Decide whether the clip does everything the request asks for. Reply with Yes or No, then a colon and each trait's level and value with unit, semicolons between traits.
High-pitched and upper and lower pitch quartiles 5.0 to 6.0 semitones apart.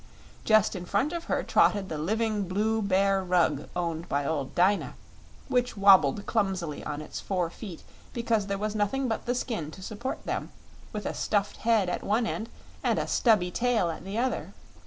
No: high, 200 Hz; average, 3.9 semitones